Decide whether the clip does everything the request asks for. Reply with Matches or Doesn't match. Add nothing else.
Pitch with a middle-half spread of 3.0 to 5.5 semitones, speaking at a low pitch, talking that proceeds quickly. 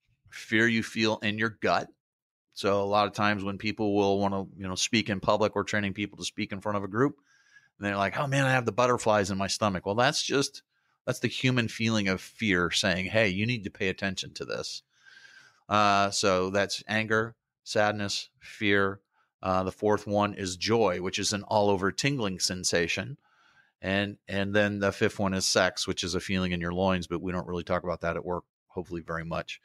Doesn't match